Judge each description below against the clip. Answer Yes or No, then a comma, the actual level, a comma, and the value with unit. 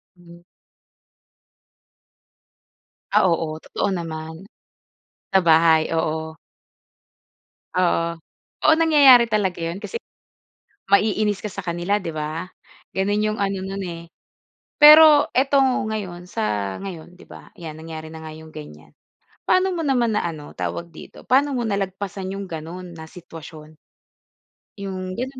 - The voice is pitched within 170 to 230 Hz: Yes, medium, 185 Hz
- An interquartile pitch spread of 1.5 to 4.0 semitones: No, average, 4.7 semitones